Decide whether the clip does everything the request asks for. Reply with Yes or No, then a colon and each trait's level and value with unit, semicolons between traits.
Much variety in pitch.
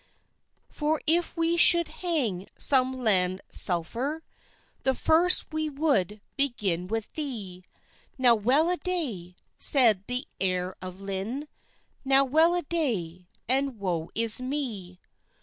Yes: wide, 8.0 semitones